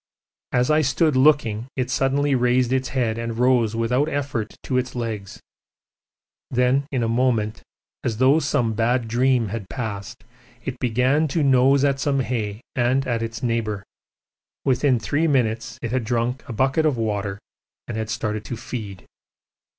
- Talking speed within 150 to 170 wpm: Yes, average, 160 wpm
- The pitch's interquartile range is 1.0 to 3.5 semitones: Yes, average, 2.8 semitones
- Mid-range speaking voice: No, low, 125 Hz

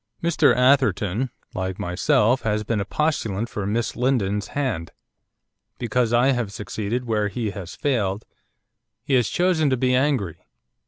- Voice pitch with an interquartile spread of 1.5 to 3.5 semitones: No, average, 4.2 semitones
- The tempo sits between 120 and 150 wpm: Yes, average, 145 wpm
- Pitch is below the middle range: Yes, low, 115 Hz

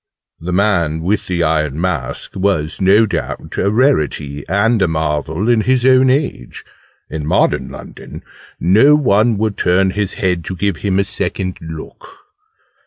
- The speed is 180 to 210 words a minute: No, average, 155 wpm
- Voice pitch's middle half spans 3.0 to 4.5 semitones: No, average, 5.0 semitones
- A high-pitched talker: No, very low, 95 Hz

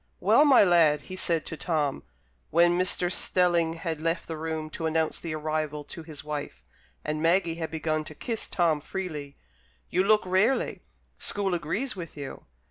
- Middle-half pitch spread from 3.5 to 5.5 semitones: No, average, 2.7 semitones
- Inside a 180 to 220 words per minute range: No, average, 170 wpm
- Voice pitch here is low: No, medium, 165 Hz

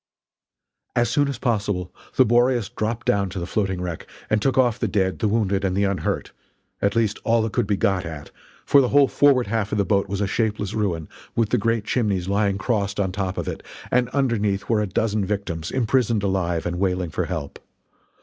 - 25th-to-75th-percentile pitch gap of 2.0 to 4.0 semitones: Yes, average, 3.3 semitones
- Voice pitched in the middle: No, low, 105 Hz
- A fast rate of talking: Yes, fast, 210 wpm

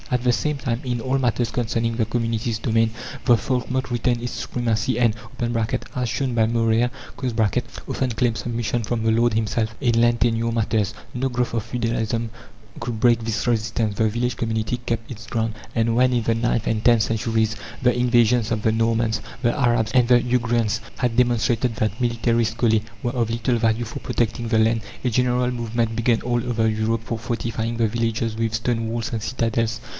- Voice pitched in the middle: No, low, 115 Hz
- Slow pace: No, average, 185 wpm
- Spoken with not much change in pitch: Yes, narrow, 1.4 semitones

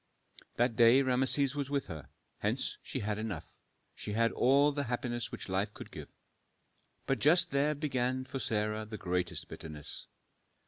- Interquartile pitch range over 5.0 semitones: No, average, 4.4 semitones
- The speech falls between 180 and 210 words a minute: No, average, 155 wpm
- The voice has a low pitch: Yes, low, 120 Hz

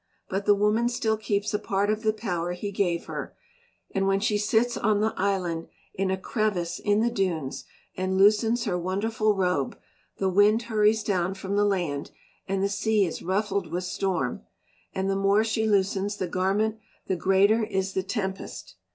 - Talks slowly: No, average, 180 wpm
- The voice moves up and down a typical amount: No, narrow, 2.2 semitones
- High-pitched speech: Yes, high, 200 Hz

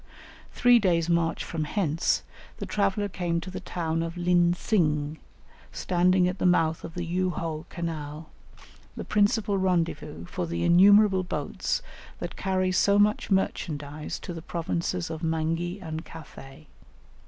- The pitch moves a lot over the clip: No, average, 2.7 semitones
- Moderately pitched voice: Yes, medium, 170 Hz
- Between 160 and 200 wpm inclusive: No, average, 145 wpm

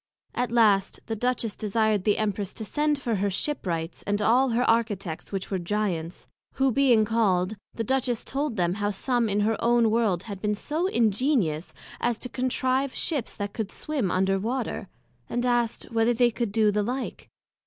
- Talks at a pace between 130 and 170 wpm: No, average, 185 wpm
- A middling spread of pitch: Yes, average, 3.4 semitones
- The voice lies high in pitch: Yes, high, 225 Hz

